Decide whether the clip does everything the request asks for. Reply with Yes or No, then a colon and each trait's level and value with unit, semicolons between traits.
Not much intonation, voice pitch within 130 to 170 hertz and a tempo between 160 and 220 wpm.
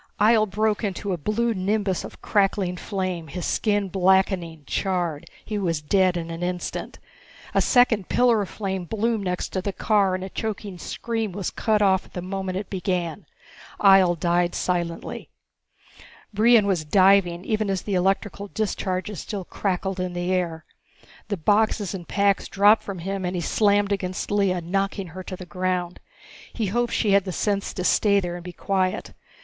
No: narrow, 2.3 semitones; high, 190 Hz; average, 175 wpm